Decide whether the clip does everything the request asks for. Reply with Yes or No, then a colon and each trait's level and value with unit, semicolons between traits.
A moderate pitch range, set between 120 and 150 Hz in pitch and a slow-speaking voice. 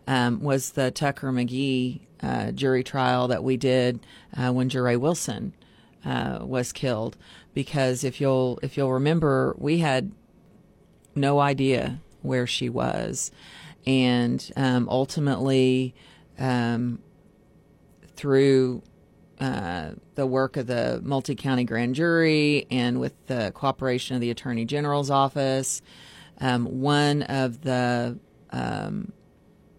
No: narrow, 1.8 semitones; low, 130 Hz; slow, 125 wpm